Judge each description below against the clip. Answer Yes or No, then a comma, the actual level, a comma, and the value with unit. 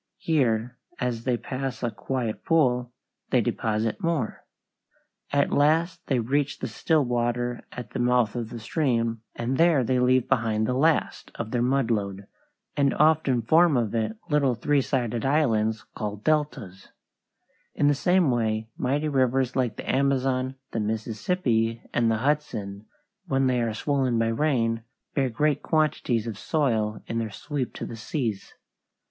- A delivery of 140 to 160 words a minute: Yes, average, 155 wpm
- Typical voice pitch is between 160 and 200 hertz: No, low, 125 Hz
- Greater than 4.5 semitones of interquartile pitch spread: No, average, 3.9 semitones